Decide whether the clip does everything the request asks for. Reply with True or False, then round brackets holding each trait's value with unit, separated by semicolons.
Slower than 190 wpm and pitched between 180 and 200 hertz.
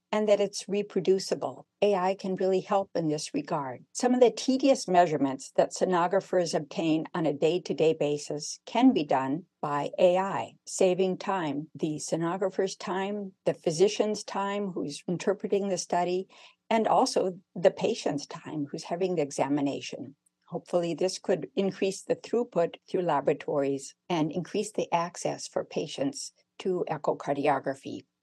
True (140 wpm; 185 Hz)